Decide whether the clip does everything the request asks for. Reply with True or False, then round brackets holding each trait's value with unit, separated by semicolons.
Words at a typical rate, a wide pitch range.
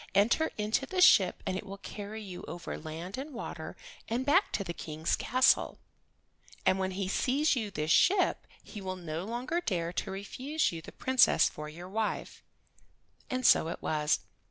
True (175 wpm; 6.6 semitones)